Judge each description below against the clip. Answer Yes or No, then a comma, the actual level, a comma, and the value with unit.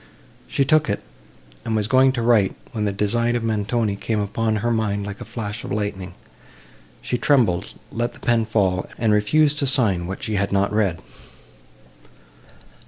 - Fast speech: No, average, 170 wpm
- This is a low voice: Yes, low, 110 Hz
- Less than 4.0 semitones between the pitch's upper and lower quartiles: Yes, average, 2.7 semitones